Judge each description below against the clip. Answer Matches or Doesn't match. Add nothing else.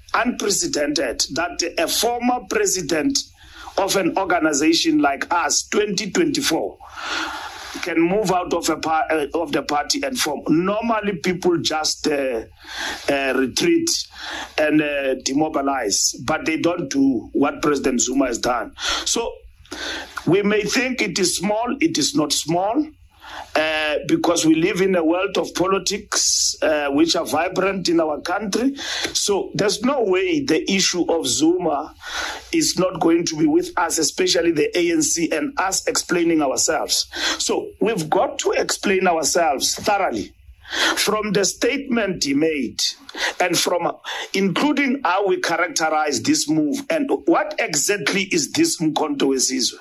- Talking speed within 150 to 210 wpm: Doesn't match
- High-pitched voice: Matches